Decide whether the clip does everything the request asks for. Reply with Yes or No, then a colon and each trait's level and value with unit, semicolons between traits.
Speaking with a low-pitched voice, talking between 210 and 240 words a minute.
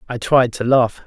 Yes: low, 125 Hz; fast, 225 wpm